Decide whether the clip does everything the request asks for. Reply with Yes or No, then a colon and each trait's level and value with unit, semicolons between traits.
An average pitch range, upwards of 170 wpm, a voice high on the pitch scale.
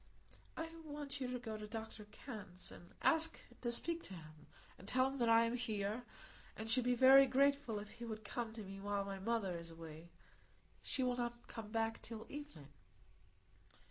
Yes: average, 3.9 semitones; average, 190 wpm; high, 225 Hz